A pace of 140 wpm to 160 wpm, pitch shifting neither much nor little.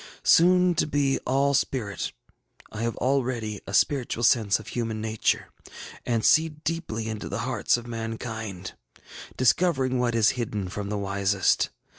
Yes: average, 145 wpm; average, 4.0 semitones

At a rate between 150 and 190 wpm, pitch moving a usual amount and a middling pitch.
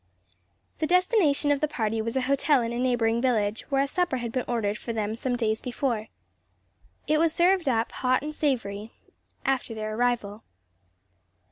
No: average, 175 wpm; average, 4.2 semitones; high, 245 Hz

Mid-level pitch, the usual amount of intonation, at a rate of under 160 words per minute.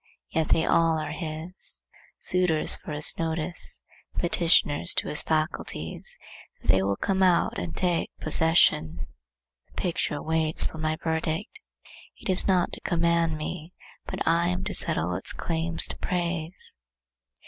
No: medium, 160 Hz; narrow, 2.0 semitones; average, 145 wpm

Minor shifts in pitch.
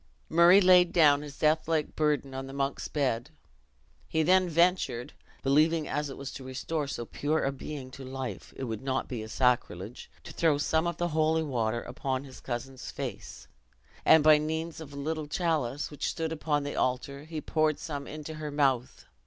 No: average, 3.1 semitones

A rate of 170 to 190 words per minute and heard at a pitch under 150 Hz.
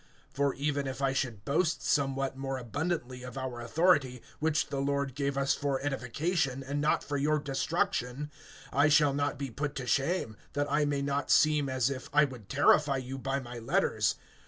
Yes: average, 185 wpm; medium, 140 Hz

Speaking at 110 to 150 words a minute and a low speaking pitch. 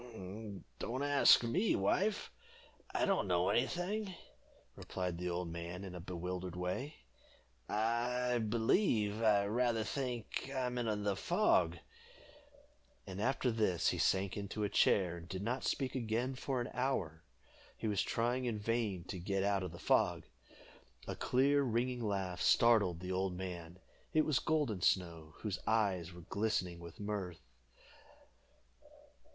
Yes: average, 145 wpm; low, 105 Hz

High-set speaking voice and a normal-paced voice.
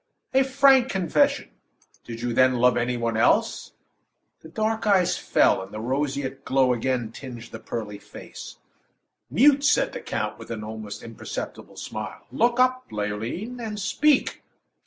No: low, 130 Hz; average, 150 wpm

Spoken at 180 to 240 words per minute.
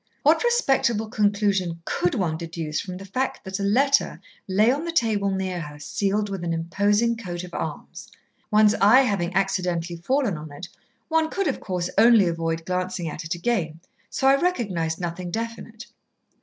No: average, 170 wpm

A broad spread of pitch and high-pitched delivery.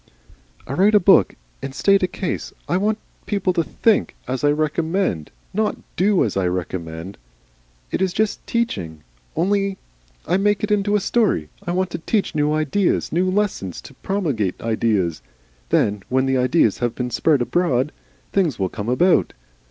No: wide, 9.0 semitones; medium, 160 Hz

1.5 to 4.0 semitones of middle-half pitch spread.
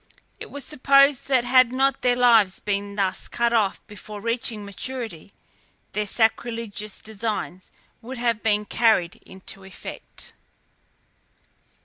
Yes: average, 3.3 semitones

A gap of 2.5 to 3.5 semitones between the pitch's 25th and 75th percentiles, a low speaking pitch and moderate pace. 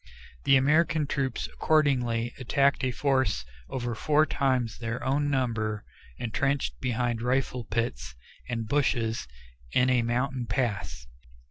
No: average, 3.0 semitones; low, 125 Hz; slow, 120 wpm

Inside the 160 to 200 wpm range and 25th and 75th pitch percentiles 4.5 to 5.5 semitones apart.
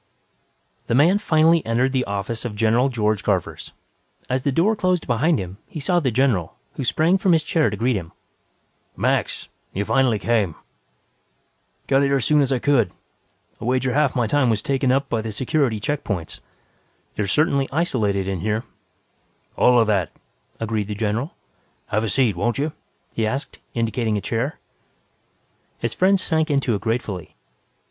Yes: average, 175 wpm; average, 4.8 semitones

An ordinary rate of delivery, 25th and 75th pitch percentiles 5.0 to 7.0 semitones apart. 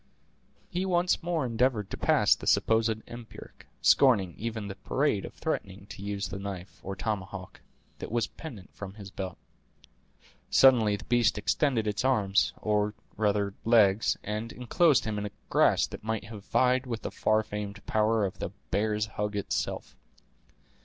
No: average, 160 wpm; average, 2.7 semitones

